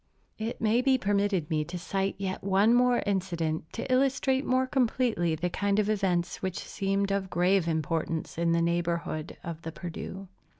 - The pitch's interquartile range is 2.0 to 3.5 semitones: No, average, 4.0 semitones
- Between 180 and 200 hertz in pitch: Yes, high, 190 Hz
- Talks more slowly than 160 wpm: No, average, 170 wpm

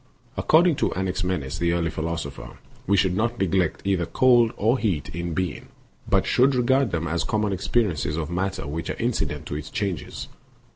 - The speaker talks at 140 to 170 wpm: No, average, 185 wpm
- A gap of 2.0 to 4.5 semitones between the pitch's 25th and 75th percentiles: No, average, 5.2 semitones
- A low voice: Yes, very low, 90 Hz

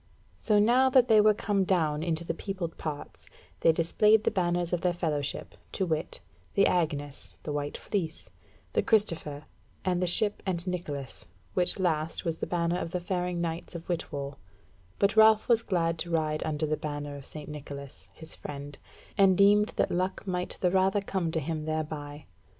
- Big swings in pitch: No, average, 3.8 semitones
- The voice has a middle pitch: Yes, medium, 170 Hz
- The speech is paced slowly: No, average, 180 wpm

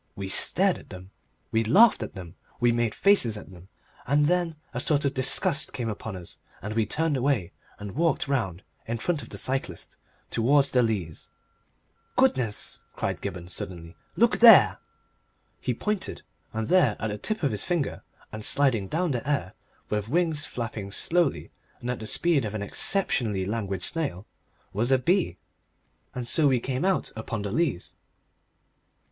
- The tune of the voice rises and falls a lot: Yes, wide, 6.2 semitones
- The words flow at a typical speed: Yes, average, 175 wpm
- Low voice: Yes, low, 120 Hz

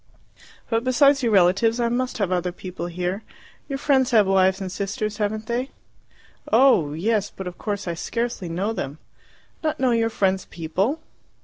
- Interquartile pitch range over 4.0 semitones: Yes, average, 4.5 semitones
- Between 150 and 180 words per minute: Yes, average, 170 wpm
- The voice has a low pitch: No, high, 210 Hz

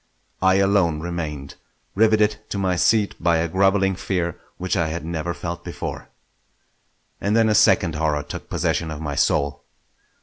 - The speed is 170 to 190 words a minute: No, average, 160 wpm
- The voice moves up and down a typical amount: Yes, average, 3.7 semitones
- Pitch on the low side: Yes, very low, 85 Hz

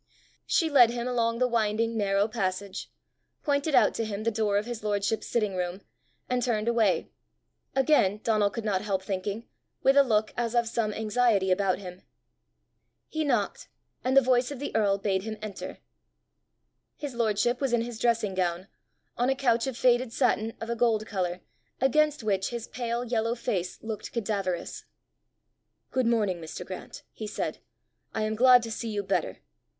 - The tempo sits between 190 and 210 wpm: No, average, 175 wpm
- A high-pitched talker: Yes, high, 225 Hz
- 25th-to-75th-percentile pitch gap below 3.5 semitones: Yes, average, 3.1 semitones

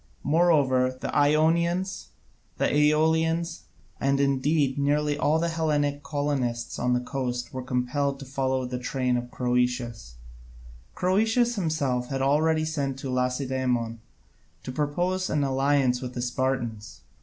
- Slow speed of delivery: Yes, slow, 130 wpm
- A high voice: No, medium, 140 Hz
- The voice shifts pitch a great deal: No, average, 3.6 semitones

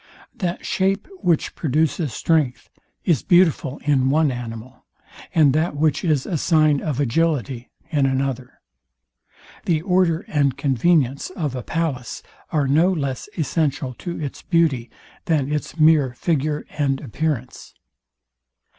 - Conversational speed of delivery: No, slow, 130 wpm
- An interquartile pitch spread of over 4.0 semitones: No, average, 3.6 semitones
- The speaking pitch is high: No, medium, 150 Hz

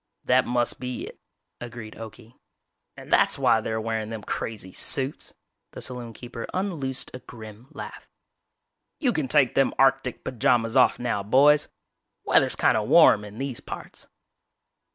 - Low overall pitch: Yes, low, 120 Hz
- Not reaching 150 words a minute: Yes, average, 140 wpm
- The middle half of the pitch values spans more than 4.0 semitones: No, average, 3.0 semitones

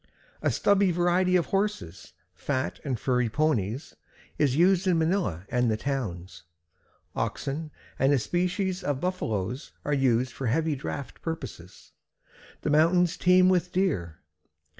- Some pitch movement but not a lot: No, wide, 6.5 semitones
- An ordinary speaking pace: No, slow, 130 wpm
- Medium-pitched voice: Yes, medium, 150 Hz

